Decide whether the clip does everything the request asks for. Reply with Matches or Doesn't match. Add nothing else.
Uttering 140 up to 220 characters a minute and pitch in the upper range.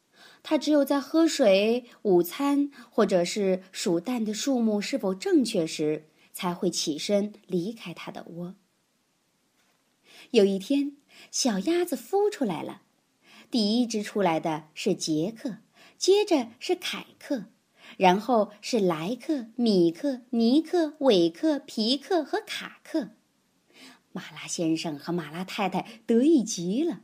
Matches